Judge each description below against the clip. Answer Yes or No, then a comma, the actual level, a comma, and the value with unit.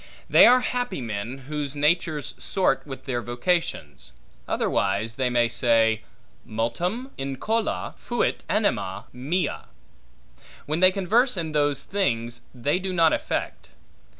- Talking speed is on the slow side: Yes, slow, 125 wpm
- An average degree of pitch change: No, wide, 7.4 semitones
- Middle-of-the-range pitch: Yes, medium, 145 Hz